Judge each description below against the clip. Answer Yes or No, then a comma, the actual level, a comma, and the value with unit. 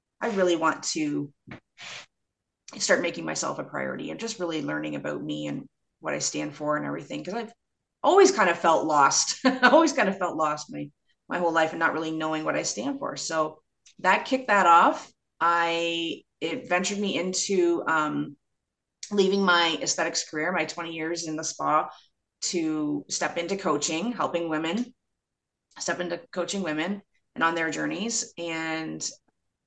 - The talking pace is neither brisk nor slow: Yes, average, 170 wpm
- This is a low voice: No, medium, 170 Hz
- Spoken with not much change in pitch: No, average, 4.1 semitones